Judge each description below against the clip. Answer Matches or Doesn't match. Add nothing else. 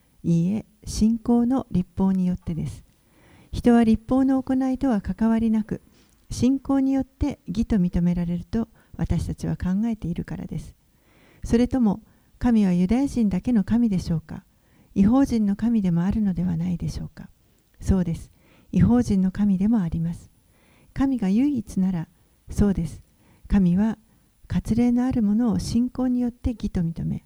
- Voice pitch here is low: Doesn't match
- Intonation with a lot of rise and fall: Doesn't match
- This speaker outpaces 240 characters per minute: Matches